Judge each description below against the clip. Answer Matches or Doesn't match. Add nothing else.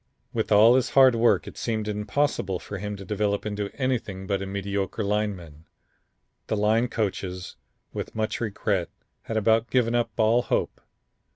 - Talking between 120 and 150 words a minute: Doesn't match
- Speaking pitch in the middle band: Doesn't match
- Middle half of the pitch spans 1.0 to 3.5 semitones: Matches